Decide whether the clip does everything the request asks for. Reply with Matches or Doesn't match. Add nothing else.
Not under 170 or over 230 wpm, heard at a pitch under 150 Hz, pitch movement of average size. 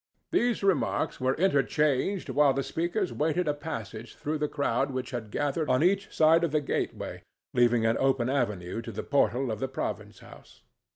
Matches